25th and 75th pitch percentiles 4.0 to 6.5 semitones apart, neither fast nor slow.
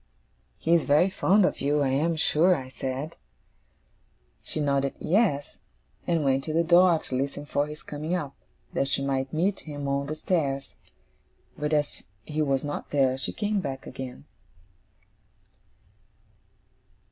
No: average, 3.2 semitones; average, 150 wpm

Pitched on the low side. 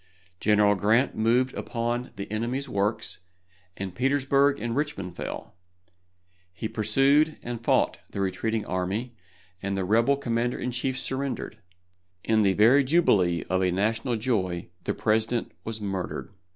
Yes: low, 110 Hz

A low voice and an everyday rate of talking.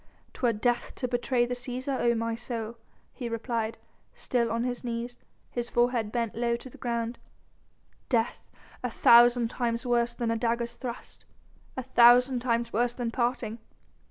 No: high, 240 Hz; average, 155 wpm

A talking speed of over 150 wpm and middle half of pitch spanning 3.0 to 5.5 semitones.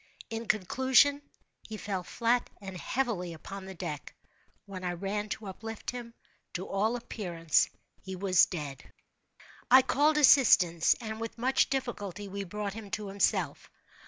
No: average, 145 wpm; average, 4.1 semitones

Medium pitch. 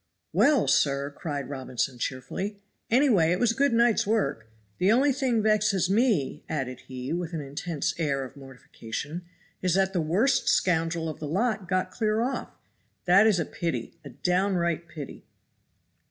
Yes: medium, 175 Hz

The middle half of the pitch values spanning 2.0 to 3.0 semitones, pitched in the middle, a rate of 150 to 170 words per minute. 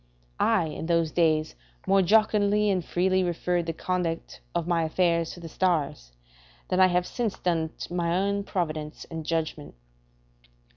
Yes: narrow, 2.4 semitones; medium, 175 Hz; average, 155 wpm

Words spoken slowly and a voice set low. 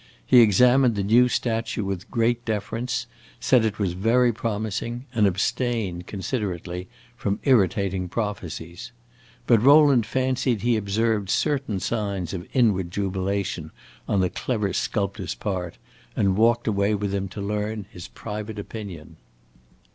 Yes: slow, 130 wpm; low, 105 Hz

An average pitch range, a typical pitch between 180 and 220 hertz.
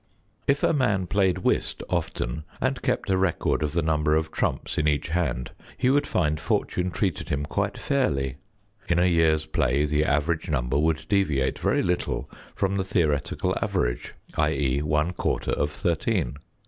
No: average, 4.0 semitones; very low, 80 Hz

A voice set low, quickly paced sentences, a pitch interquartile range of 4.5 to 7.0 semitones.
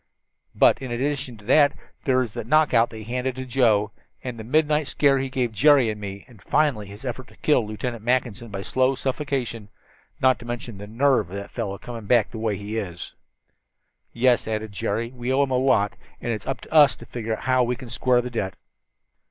No: low, 120 Hz; fast, 225 wpm; average, 3.3 semitones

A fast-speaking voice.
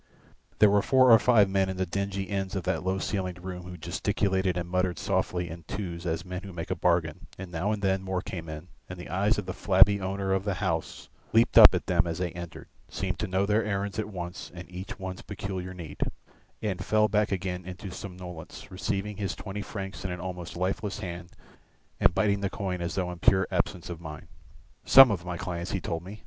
Yes: fast, 220 wpm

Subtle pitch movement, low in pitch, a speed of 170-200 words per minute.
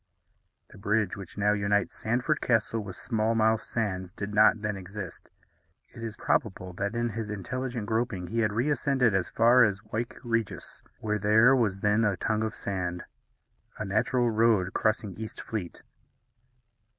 No: narrow, 2.3 semitones; low, 110 Hz; average, 155 wpm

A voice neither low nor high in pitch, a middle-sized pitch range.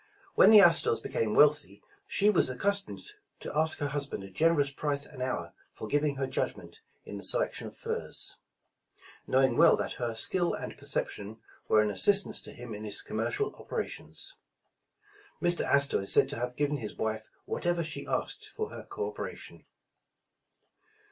No: medium, 145 Hz; wide, 7.1 semitones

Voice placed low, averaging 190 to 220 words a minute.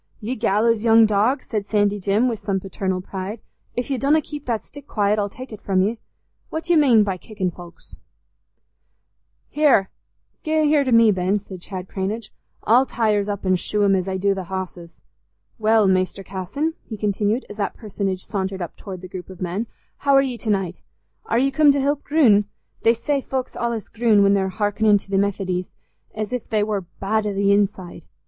No: high, 205 Hz; fast, 205 wpm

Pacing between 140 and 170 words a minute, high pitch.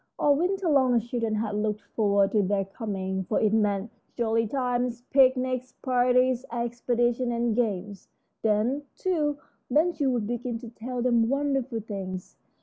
Yes: average, 150 wpm; high, 240 Hz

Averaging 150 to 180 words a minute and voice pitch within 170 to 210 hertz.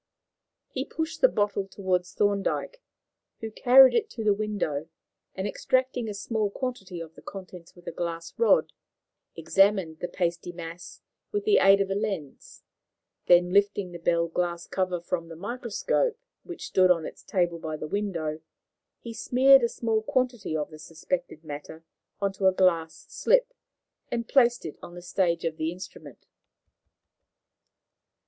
Yes: average, 160 wpm; high, 190 Hz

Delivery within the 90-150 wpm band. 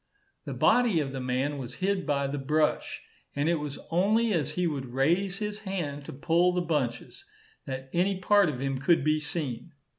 No: average, 190 wpm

